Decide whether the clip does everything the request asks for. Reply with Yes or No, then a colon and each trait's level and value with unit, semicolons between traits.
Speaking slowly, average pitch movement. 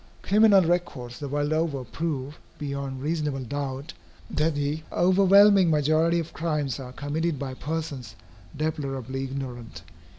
Yes: slow, 125 wpm; average, 3.4 semitones